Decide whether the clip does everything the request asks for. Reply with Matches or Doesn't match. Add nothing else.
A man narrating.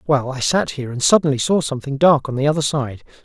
Matches